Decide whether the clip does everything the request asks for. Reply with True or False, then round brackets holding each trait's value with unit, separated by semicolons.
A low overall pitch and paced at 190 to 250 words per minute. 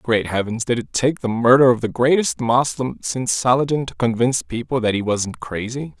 True (120 Hz; 200 wpm)